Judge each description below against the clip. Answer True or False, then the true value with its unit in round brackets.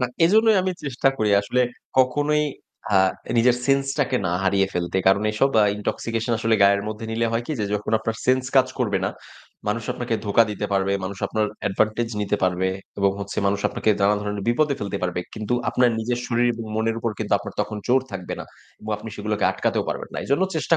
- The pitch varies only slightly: False (3.8 semitones)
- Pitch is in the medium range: False (110 Hz)